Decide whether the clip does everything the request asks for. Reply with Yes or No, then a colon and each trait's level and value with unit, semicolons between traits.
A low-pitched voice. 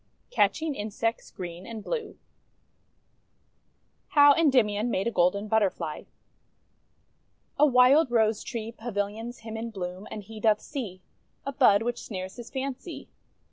No: high, 225 Hz